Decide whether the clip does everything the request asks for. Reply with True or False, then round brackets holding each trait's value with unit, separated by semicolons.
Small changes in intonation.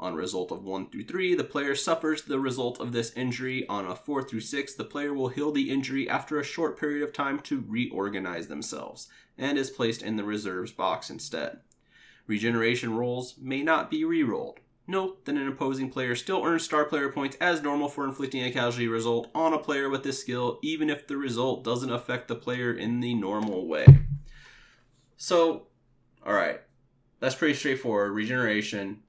False (3.6 semitones)